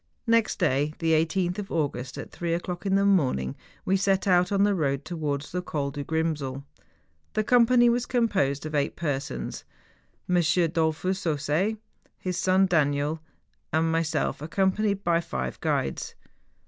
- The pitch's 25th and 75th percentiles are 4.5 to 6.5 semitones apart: Yes, average, 4.8 semitones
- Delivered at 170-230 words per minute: No, average, 150 wpm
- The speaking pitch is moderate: Yes, medium, 165 Hz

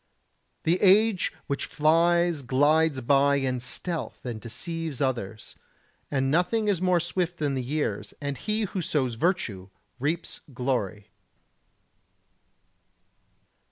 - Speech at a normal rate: No, slow, 115 wpm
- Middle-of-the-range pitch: Yes, medium, 150 Hz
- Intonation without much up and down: No, average, 5.1 semitones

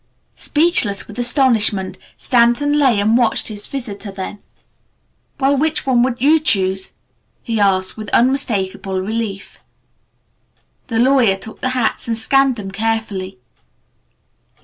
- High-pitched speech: Yes, high, 225 Hz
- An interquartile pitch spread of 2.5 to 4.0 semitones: No, average, 4.5 semitones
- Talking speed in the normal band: No, slow, 125 wpm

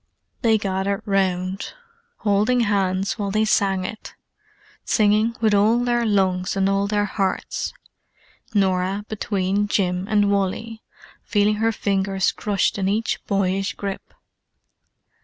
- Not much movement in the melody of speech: Yes, narrow, 1.8 semitones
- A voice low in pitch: No, high, 200 Hz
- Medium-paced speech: No, slow, 120 wpm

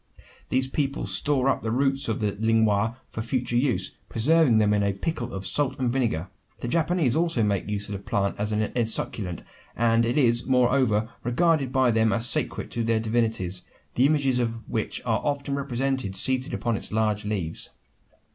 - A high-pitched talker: No, low, 115 Hz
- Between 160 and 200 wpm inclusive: Yes, average, 185 wpm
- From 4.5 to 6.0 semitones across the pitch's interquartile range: No, average, 3.7 semitones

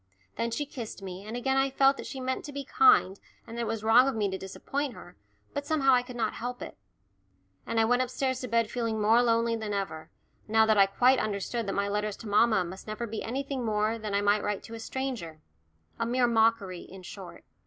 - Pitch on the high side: Yes, high, 230 Hz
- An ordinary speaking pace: No, fast, 235 wpm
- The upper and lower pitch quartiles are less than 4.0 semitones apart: Yes, average, 3.4 semitones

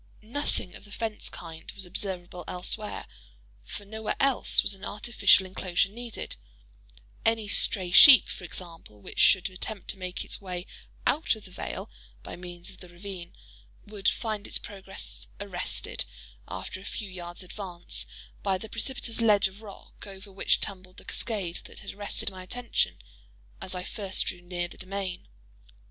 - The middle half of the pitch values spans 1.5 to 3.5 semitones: Yes, average, 2.8 semitones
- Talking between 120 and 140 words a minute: No, average, 160 wpm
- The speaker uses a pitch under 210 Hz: Yes, high, 190 Hz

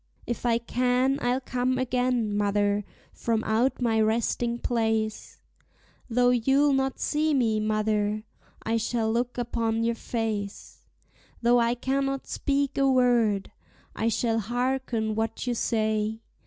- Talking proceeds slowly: Yes, slow, 130 wpm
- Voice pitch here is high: Yes, high, 235 Hz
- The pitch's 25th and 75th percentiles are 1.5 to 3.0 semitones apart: Yes, narrow, 2.4 semitones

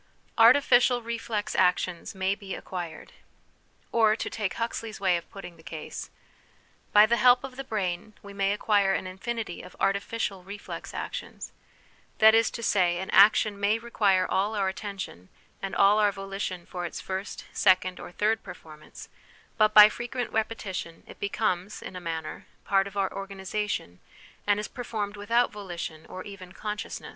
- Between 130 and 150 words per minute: No, average, 165 wpm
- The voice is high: Yes, high, 200 Hz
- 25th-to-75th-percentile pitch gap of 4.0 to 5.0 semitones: No, average, 2.7 semitones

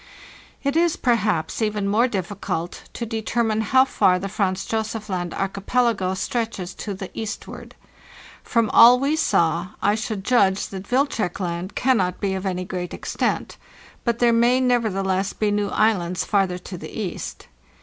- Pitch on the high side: Yes, high, 205 Hz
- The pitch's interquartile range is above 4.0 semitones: No, average, 3.7 semitones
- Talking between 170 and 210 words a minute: No, average, 155 wpm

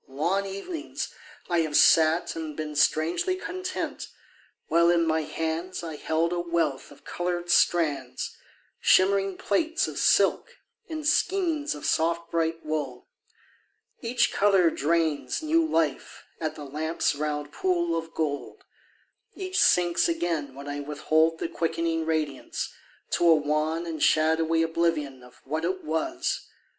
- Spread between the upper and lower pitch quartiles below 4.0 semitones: Yes, average, 2.9 semitones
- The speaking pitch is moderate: Yes, medium, 165 Hz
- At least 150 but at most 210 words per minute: No, slow, 135 wpm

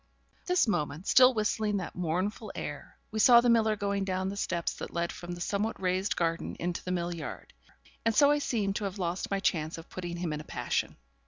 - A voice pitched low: No, high, 190 Hz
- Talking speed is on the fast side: Yes, fast, 230 wpm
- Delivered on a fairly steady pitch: No, average, 3.7 semitones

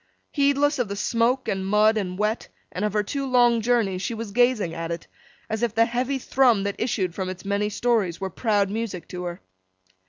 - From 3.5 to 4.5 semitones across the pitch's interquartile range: Yes, average, 3.9 semitones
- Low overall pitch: No, high, 215 Hz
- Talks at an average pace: No, fast, 210 wpm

